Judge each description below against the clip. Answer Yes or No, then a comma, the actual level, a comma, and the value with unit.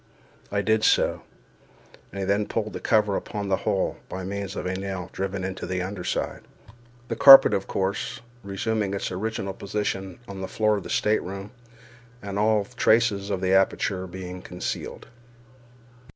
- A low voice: Yes, low, 100 Hz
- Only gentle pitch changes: Yes, narrow, 2.0 semitones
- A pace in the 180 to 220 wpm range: No, average, 160 wpm